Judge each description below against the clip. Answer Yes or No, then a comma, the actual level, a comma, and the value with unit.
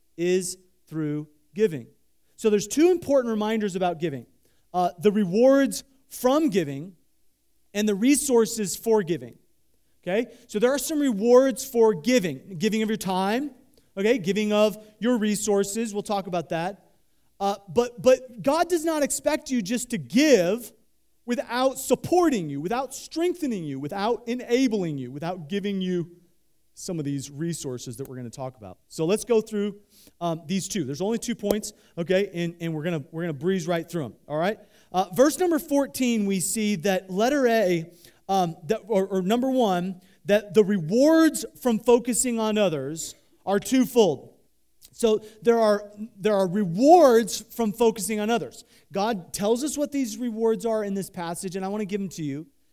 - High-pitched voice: Yes, high, 210 Hz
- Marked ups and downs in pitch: No, average, 5.0 semitones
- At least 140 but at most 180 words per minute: Yes, average, 175 wpm